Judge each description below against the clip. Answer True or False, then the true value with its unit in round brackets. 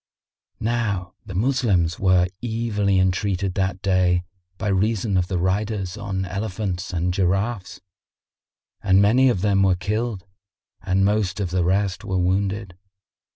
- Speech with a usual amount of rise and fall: False (2.2 semitones)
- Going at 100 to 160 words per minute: True (140 wpm)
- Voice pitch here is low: True (95 Hz)